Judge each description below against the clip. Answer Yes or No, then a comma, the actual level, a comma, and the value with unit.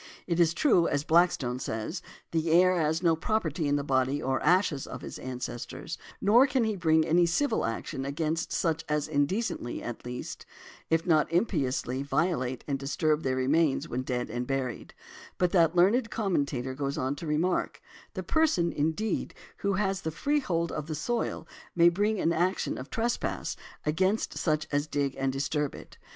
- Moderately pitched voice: Yes, medium, 160 Hz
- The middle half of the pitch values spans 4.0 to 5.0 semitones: Yes, average, 4.7 semitones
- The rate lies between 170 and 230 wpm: Yes, average, 175 wpm